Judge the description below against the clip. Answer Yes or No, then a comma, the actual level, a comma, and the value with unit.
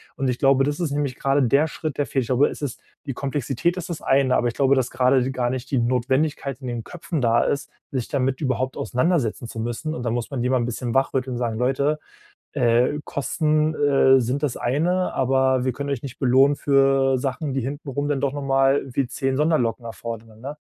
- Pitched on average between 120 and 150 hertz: Yes, low, 135 Hz